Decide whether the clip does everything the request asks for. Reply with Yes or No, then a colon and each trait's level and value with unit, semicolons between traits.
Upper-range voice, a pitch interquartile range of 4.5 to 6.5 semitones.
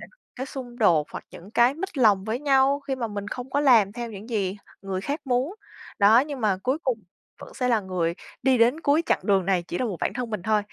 Yes: high, 235 Hz; average, 4.8 semitones